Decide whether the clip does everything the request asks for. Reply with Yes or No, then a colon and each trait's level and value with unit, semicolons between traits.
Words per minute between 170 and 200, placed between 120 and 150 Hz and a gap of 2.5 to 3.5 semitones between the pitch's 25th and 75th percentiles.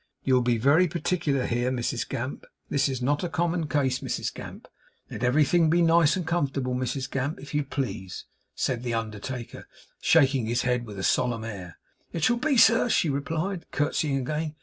No: average, 185 wpm; low, 135 Hz; average, 4.5 semitones